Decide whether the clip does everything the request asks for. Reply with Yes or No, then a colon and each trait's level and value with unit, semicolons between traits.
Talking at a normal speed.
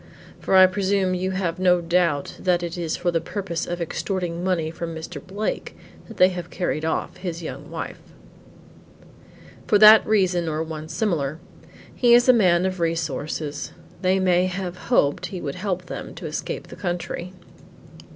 Yes: average, 170 wpm